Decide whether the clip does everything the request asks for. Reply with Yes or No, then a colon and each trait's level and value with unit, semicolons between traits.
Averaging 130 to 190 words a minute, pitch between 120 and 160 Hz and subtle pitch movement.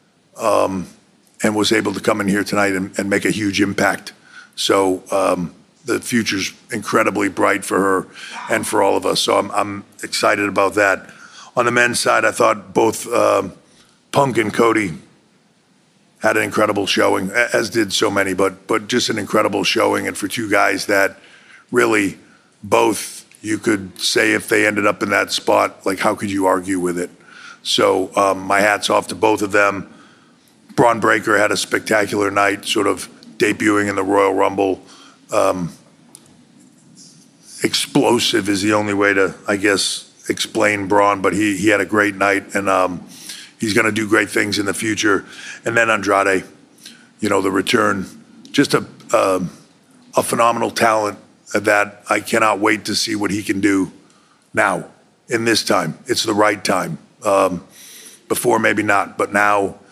No: average, 170 wpm; low, 100 Hz; narrow, 1.2 semitones